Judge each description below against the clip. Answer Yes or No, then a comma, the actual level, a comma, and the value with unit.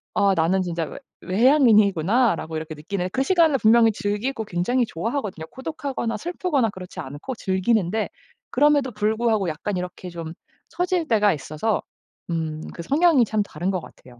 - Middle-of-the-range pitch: No, high, 210 Hz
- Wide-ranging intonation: Yes, wide, 6.5 semitones